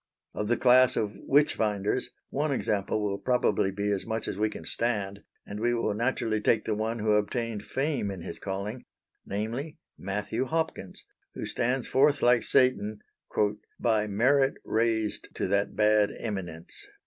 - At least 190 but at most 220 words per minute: No, average, 155 wpm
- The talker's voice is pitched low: Yes, low, 110 Hz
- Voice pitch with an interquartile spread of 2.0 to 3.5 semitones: Yes, average, 3.2 semitones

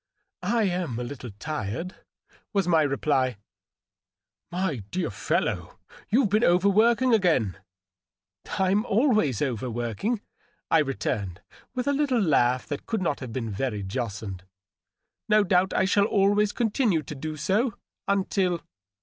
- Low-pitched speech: No, medium, 175 Hz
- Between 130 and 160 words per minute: Yes, average, 140 wpm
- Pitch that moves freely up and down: Yes, wide, 8.3 semitones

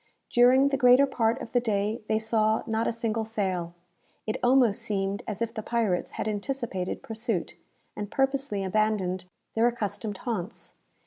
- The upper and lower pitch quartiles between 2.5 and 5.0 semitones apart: Yes, average, 2.9 semitones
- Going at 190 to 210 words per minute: No, average, 155 wpm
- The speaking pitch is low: No, high, 220 Hz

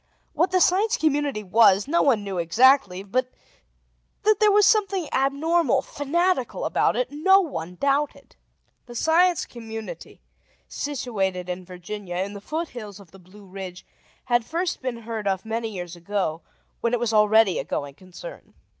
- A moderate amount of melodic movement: No, wide, 8.4 semitones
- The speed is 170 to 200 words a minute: No, average, 155 wpm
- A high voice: Yes, high, 230 Hz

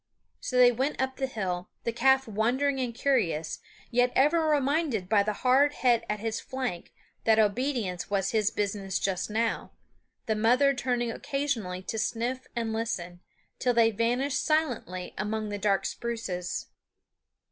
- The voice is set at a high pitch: Yes, high, 230 Hz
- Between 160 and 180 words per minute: No, average, 150 wpm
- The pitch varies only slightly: No, average, 4.1 semitones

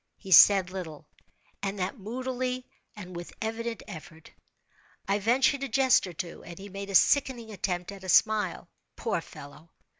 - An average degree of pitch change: Yes, average, 4.4 semitones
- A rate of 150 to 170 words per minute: Yes, average, 160 wpm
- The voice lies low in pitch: No, high, 200 Hz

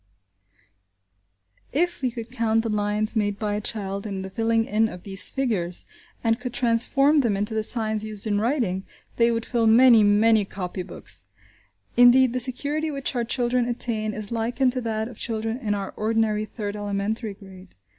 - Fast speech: No, average, 175 wpm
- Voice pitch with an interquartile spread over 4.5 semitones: No, average, 2.7 semitones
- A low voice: No, high, 225 Hz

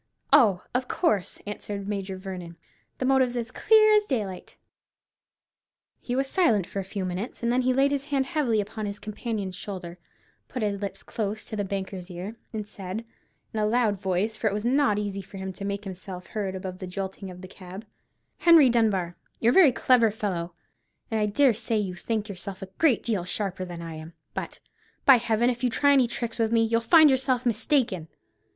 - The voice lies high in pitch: Yes, high, 210 Hz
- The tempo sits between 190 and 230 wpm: Yes, average, 200 wpm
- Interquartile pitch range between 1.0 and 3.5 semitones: No, average, 4.3 semitones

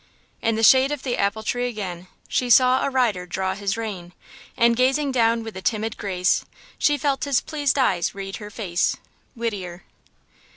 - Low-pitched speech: No, high, 225 Hz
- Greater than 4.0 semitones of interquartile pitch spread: Yes, average, 4.8 semitones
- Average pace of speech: Yes, average, 175 wpm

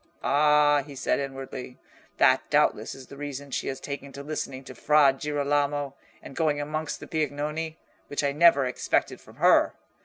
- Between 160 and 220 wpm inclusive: Yes, average, 165 wpm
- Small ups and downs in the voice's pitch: Yes, narrow, 1.5 semitones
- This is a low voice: No, medium, 145 Hz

